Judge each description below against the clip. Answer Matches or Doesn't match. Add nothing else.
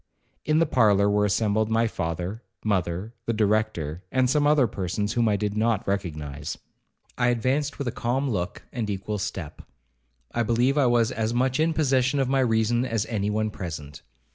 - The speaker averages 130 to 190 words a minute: Matches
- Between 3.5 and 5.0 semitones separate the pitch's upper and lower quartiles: Matches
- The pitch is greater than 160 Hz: Doesn't match